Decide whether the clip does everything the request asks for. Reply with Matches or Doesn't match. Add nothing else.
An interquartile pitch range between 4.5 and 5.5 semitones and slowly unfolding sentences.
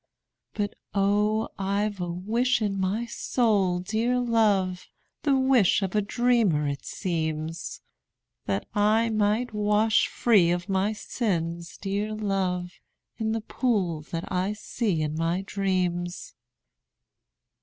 Doesn't match